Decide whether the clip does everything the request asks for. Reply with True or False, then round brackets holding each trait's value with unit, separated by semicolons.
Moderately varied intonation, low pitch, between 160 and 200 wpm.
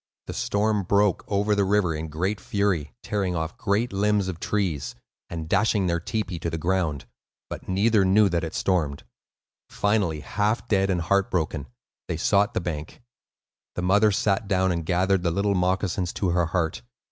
True (3.3 semitones; 95 Hz; 175 wpm)